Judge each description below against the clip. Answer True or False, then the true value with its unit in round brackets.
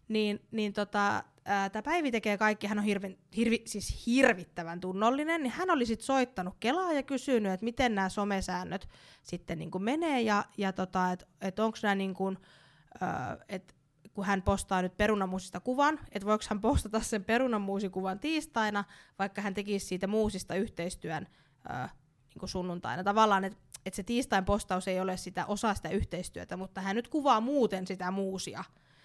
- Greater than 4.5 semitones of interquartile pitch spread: False (3.0 semitones)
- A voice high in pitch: True (200 Hz)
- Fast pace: True (160 wpm)